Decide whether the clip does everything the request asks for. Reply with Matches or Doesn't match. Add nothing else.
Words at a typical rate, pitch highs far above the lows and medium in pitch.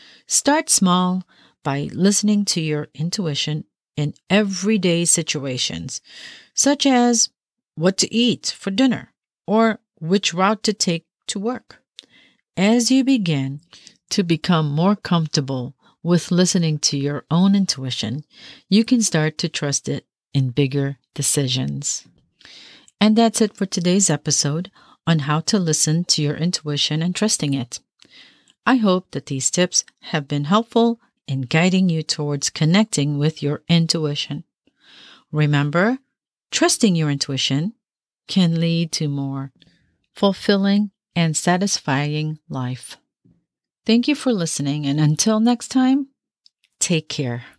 Doesn't match